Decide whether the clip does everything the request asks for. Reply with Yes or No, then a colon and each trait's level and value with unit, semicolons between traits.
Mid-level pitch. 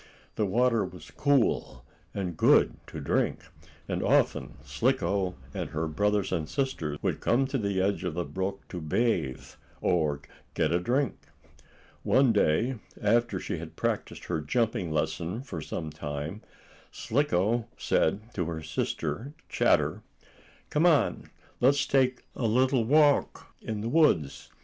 No: low, 105 Hz